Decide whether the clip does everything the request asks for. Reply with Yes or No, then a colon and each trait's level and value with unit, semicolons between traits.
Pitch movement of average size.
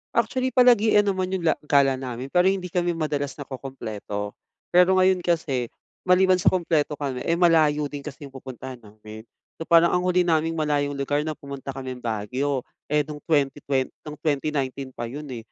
Yes: average, 4.7 semitones